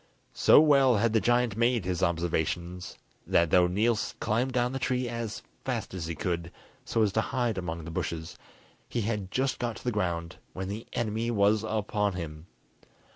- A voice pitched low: Yes, low, 105 Hz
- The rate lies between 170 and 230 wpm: Yes, average, 180 wpm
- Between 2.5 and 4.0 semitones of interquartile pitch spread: No, average, 5.0 semitones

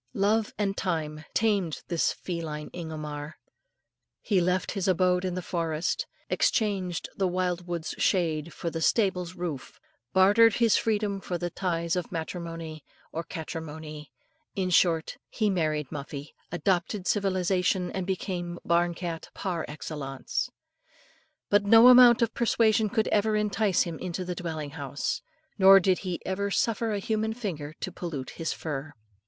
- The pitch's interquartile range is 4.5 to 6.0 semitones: No, average, 3.5 semitones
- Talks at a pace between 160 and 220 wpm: No, average, 145 wpm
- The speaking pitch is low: No, medium, 180 Hz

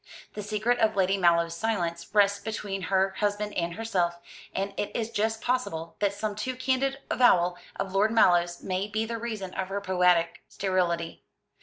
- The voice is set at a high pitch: Yes, high, 200 Hz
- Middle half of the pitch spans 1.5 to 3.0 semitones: No, average, 3.4 semitones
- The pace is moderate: Yes, average, 170 wpm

